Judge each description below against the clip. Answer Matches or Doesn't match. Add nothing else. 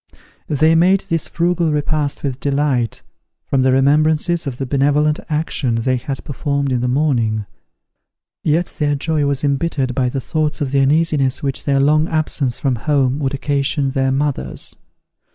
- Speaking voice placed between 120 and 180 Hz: Matches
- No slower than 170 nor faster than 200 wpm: Doesn't match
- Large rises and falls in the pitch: Doesn't match